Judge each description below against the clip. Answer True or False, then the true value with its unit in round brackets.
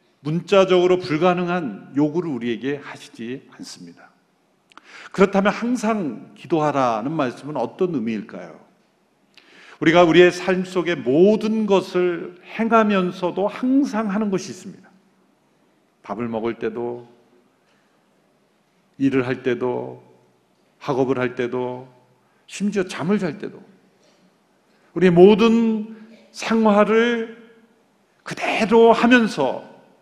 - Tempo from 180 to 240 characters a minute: True (220 characters per minute)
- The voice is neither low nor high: True (180 Hz)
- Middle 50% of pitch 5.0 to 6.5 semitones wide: False (8.8 semitones)